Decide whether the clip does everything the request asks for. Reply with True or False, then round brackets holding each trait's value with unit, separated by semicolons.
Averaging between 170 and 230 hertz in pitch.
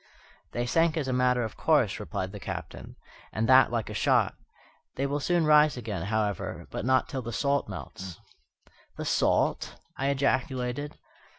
False (130 Hz)